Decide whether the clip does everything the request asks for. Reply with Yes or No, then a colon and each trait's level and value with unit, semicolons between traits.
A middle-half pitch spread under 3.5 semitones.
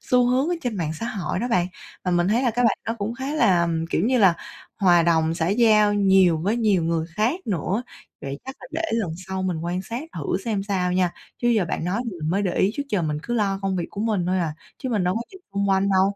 No: average, 4.5 semitones